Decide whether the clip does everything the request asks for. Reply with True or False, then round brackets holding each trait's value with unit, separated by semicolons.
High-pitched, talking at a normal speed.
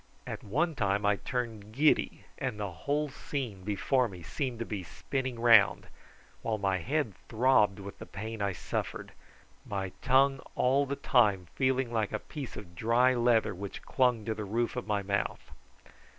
False (115 Hz; 170 wpm)